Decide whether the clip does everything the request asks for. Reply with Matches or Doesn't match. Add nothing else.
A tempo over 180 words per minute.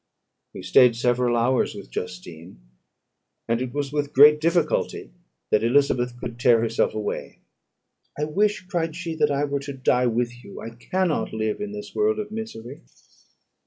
Doesn't match